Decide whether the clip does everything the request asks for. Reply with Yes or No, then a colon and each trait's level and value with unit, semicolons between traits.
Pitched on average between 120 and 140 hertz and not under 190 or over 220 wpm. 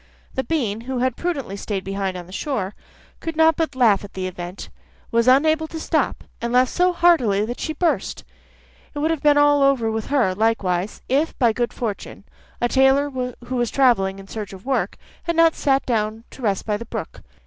No: high, 245 Hz; fast, 205 wpm